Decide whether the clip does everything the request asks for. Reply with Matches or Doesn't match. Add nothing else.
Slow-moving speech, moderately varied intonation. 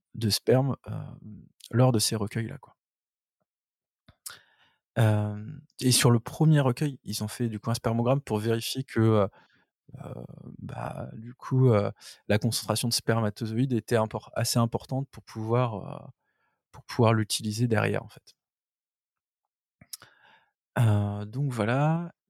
Matches